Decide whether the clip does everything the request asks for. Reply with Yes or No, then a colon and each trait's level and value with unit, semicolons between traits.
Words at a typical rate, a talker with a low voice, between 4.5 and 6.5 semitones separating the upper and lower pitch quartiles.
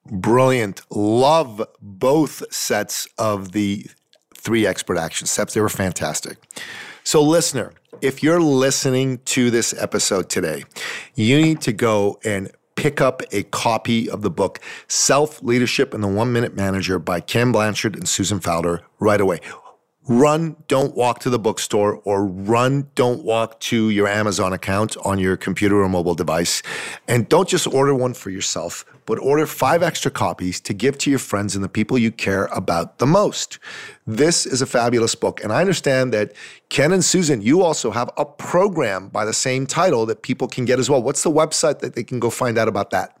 Yes: average, 185 wpm; low, 120 Hz; average, 4.9 semitones